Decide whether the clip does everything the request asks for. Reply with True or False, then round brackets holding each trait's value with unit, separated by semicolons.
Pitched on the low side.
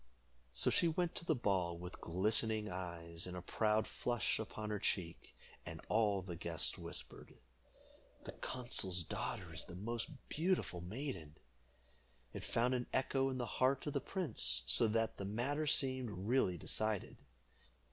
True (110 Hz)